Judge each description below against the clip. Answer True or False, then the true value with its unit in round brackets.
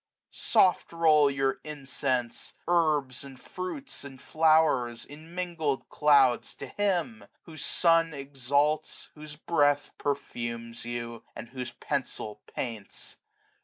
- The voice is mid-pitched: True (145 Hz)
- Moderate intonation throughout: True (3.8 semitones)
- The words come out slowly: True (100 wpm)